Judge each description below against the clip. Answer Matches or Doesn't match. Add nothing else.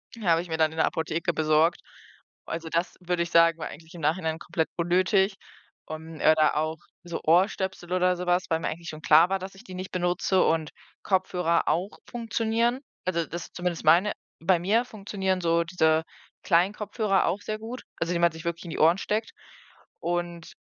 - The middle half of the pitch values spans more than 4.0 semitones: Doesn't match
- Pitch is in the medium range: Matches